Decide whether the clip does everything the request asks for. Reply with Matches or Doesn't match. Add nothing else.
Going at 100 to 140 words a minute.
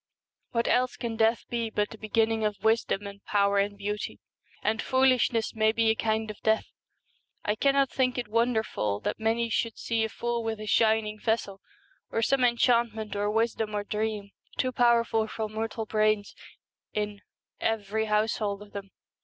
Doesn't match